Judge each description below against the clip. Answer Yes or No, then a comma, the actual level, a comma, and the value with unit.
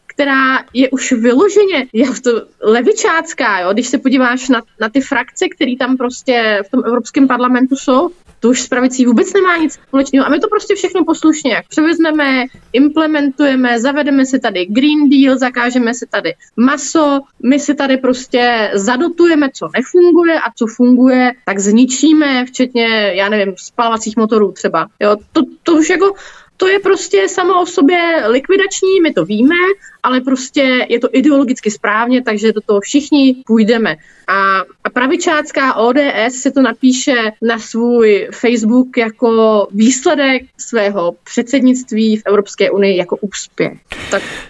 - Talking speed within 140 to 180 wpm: Yes, average, 150 wpm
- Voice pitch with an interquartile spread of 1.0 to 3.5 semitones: No, average, 4.2 semitones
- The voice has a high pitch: Yes, very high, 255 Hz